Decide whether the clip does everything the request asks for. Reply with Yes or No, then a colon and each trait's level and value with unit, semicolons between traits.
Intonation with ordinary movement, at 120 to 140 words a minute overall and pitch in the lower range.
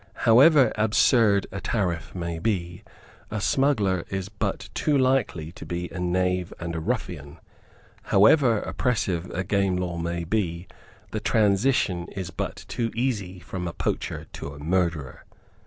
No: average, 4.2 semitones; average, 150 wpm; very low, 95 Hz